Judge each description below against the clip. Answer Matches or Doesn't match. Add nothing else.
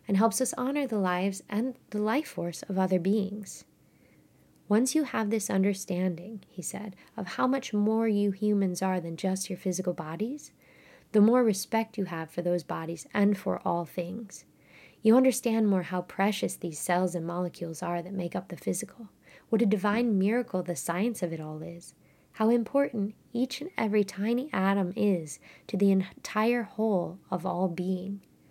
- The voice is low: Doesn't match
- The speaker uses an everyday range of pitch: Matches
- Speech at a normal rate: Matches